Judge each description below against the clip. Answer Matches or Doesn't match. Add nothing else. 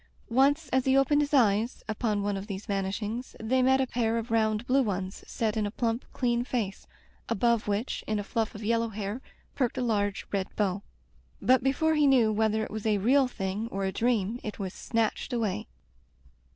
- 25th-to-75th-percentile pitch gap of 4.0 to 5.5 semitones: Doesn't match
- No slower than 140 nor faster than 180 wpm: Doesn't match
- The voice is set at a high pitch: Matches